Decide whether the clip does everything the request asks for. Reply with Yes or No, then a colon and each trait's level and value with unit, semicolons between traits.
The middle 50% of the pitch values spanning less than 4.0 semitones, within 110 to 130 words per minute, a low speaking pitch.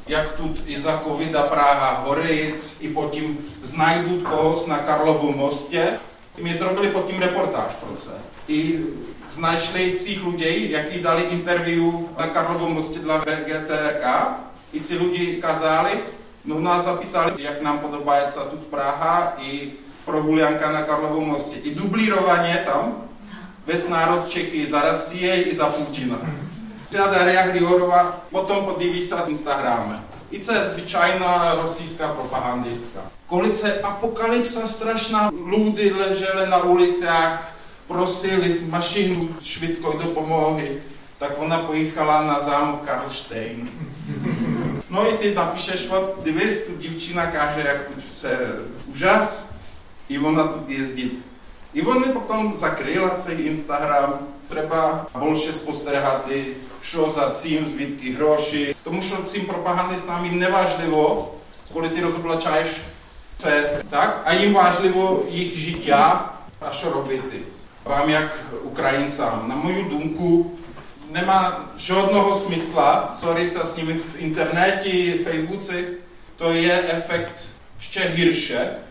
No: average, 3.2 semitones; average, 125 wpm; medium, 165 Hz